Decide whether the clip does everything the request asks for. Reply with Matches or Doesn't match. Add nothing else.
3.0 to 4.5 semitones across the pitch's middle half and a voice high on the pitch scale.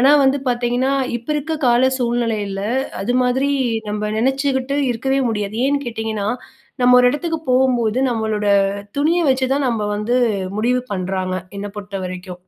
Matches